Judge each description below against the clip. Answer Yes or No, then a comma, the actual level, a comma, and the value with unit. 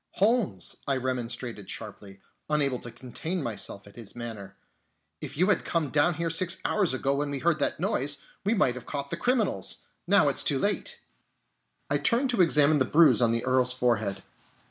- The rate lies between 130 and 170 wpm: No, average, 190 wpm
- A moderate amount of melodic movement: No, wide, 5.9 semitones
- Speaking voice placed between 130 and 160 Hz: Yes, medium, 140 Hz